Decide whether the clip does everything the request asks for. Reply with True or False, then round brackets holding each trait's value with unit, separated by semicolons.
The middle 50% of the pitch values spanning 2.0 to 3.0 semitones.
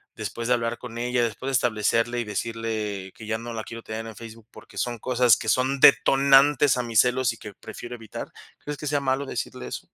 True (2.4 semitones)